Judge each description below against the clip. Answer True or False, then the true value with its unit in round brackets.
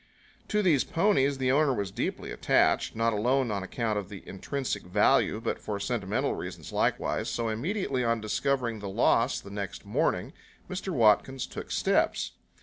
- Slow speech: False (160 wpm)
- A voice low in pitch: True (115 Hz)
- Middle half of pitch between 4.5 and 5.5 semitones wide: True (4.8 semitones)